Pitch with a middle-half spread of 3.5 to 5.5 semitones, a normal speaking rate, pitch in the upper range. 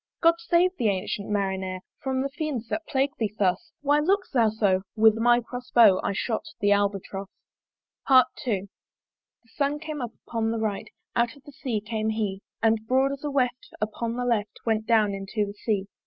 Yes: average, 4.4 semitones; average, 190 wpm; high, 225 Hz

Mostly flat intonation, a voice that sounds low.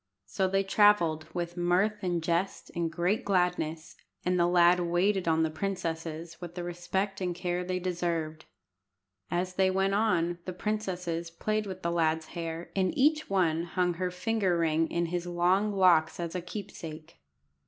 No: narrow, 2.1 semitones; medium, 175 Hz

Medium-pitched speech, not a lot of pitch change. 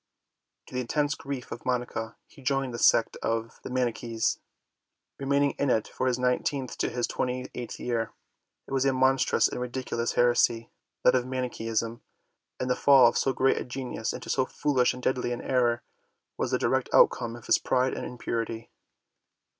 No: low, 125 Hz; narrow, 1.8 semitones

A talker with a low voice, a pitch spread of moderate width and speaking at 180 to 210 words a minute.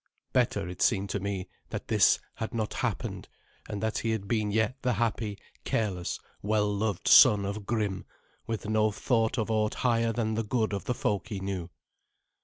No: low, 110 Hz; narrow, 1.9 semitones; average, 185 wpm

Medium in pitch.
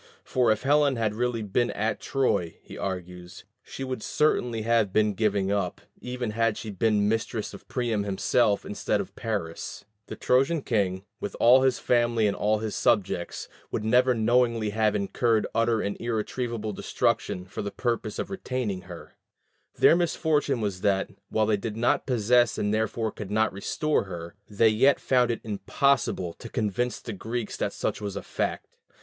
No: low, 110 Hz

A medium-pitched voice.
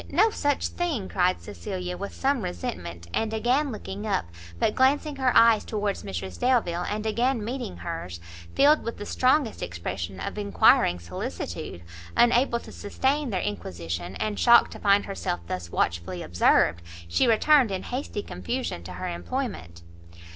No: high, 200 Hz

